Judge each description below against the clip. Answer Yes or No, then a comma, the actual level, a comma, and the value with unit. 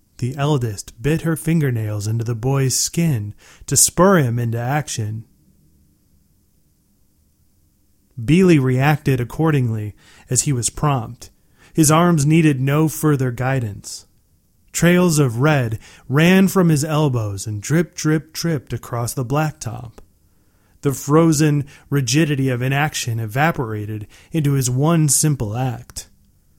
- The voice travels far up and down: Yes, wide, 6.3 semitones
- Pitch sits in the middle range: No, low, 130 Hz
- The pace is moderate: No, slow, 115 wpm